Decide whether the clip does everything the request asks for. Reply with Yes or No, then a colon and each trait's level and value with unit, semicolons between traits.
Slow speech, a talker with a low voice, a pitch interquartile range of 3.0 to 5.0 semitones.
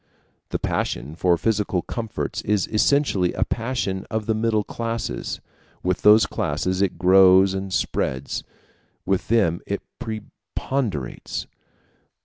Yes: slow, 120 wpm; low, 100 Hz; average, 3.5 semitones